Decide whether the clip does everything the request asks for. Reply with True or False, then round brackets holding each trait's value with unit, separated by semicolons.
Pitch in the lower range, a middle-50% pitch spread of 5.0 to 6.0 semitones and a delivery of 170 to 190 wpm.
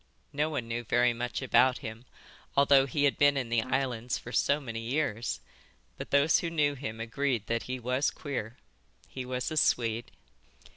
False (125 Hz; 3.3 semitones; 180 wpm)